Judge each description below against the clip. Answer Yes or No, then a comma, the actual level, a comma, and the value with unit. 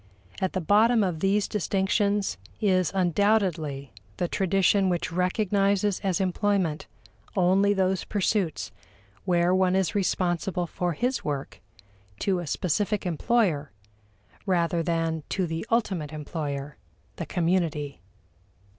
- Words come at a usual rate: No, slow, 115 wpm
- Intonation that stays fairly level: No, average, 3.3 semitones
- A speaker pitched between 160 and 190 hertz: Yes, medium, 185 Hz